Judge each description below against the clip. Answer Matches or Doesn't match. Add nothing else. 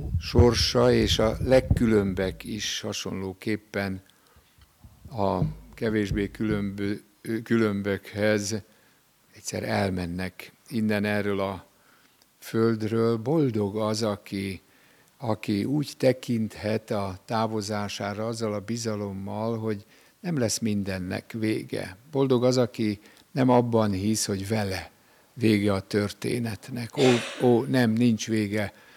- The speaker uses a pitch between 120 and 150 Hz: Doesn't match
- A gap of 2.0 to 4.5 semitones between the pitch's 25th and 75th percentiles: Matches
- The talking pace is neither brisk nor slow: Doesn't match